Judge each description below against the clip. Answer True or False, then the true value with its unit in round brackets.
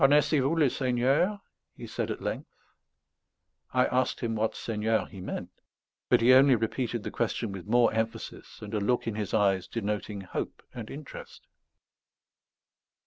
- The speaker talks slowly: False (155 wpm)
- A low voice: True (115 Hz)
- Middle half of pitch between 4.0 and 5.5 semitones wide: False (3.5 semitones)